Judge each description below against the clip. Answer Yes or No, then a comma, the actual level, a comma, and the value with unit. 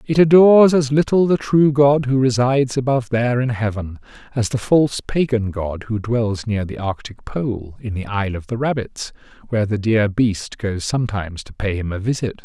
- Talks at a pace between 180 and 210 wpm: Yes, average, 200 wpm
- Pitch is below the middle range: Yes, low, 120 Hz